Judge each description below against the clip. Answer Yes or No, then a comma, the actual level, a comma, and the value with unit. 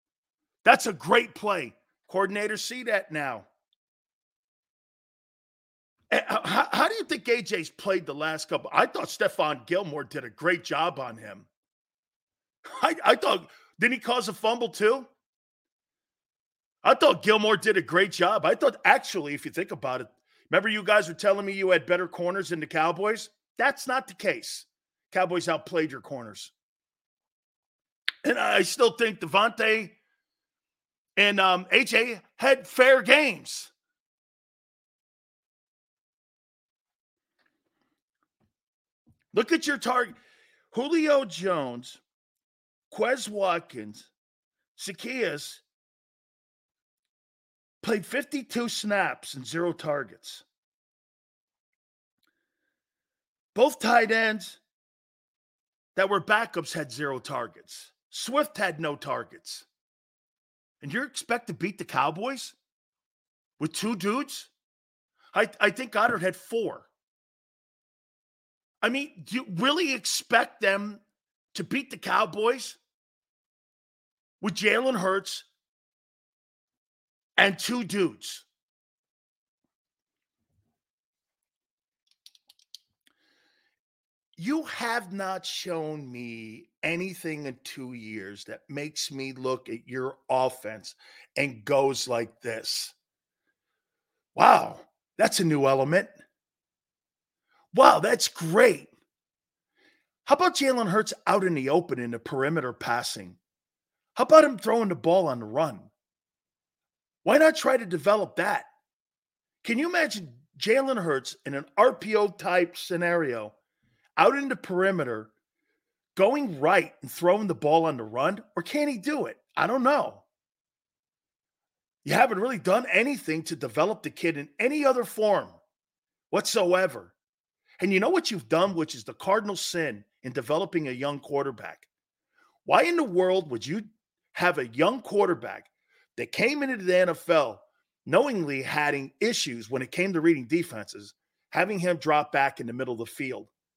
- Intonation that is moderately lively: No, wide, 7.5 semitones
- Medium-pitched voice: No, high, 195 Hz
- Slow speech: Yes, slow, 125 wpm